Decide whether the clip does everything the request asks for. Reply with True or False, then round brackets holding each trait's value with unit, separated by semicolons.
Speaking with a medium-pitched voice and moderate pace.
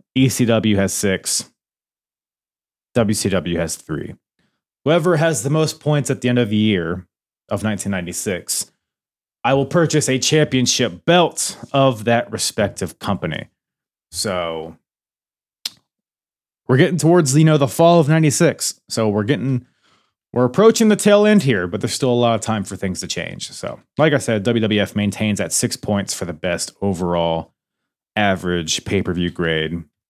False (115 Hz; 150 wpm)